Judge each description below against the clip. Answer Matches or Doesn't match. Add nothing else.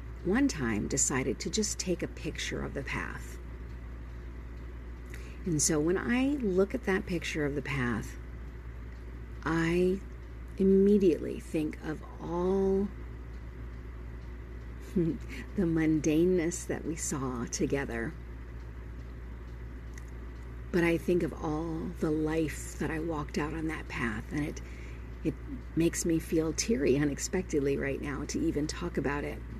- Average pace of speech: Doesn't match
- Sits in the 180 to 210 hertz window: Doesn't match